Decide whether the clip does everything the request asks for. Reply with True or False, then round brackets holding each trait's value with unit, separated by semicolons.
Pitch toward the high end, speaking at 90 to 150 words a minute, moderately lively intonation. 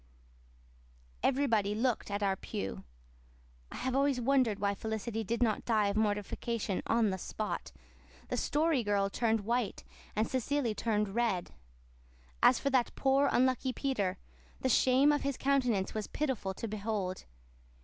True (225 Hz; 145 wpm; 4.1 semitones)